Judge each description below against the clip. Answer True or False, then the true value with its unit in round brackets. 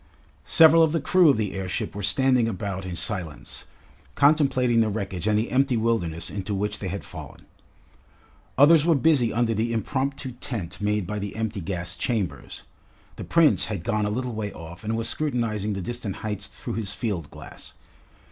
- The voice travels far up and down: False (4.3 semitones)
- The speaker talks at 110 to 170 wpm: False (180 wpm)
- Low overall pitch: True (110 Hz)